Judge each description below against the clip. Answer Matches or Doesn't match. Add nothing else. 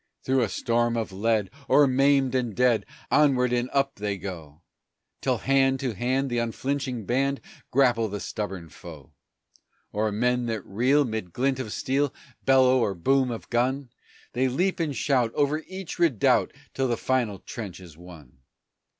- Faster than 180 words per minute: Doesn't match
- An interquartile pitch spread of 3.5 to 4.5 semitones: Matches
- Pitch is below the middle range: Matches